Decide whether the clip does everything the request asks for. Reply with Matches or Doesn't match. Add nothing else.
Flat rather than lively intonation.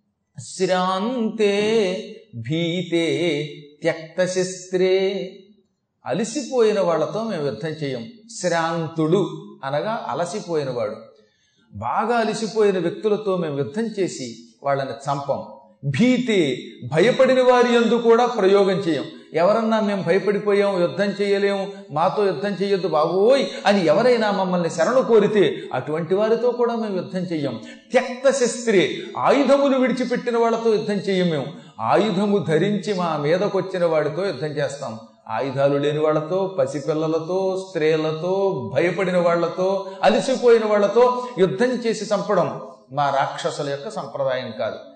Doesn't match